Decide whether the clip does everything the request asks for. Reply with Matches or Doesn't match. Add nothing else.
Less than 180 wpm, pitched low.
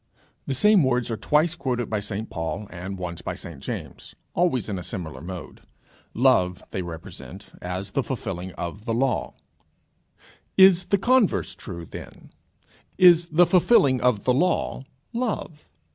Matches